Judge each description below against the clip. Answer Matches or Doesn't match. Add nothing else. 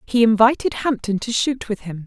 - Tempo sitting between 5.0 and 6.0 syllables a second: Matches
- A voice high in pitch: Matches